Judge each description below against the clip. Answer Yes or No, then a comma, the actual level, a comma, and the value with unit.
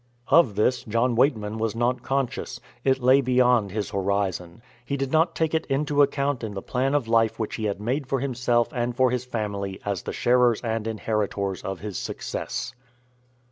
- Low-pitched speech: Yes, low, 120 Hz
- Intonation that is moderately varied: Yes, average, 3.8 semitones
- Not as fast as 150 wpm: No, average, 180 wpm